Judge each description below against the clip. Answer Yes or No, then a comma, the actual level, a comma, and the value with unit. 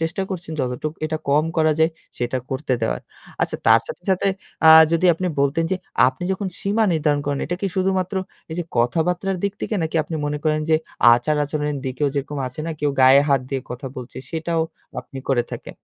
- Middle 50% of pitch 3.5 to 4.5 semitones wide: Yes, average, 4.0 semitones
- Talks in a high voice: No, medium, 155 Hz